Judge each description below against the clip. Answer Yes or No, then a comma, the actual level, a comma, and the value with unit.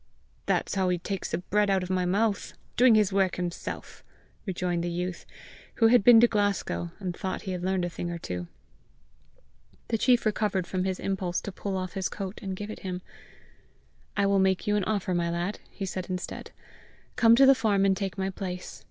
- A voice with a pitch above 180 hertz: Yes, high, 190 Hz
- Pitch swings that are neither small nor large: No, narrow, 2.3 semitones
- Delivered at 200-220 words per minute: Yes, fast, 205 wpm